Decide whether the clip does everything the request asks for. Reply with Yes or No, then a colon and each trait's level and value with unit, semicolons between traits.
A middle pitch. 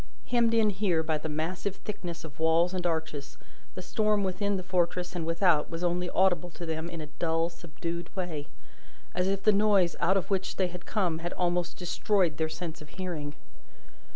Yes: medium, 175 Hz